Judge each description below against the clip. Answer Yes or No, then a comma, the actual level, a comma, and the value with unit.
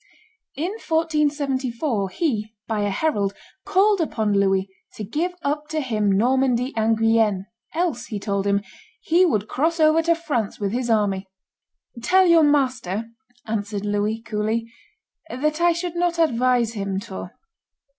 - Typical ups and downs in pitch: No, wide, 7.0 semitones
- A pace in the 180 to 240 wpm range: No, average, 145 wpm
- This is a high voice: Yes, high, 240 Hz